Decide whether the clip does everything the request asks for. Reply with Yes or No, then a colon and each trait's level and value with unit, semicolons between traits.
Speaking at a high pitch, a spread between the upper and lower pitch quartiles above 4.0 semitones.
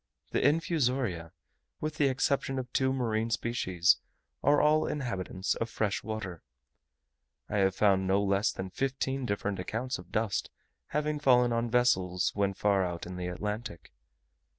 No: low, 110 Hz; wide, 5.6 semitones